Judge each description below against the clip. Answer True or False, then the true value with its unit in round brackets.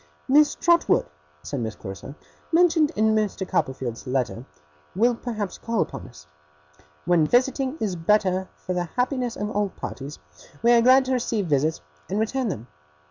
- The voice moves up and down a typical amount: False (7.9 semitones)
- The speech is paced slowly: False (155 wpm)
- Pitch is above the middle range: True (210 Hz)